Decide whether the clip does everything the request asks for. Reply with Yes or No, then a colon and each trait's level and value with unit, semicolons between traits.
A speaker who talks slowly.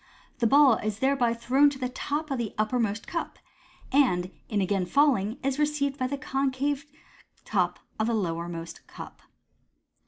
No: average, 165 wpm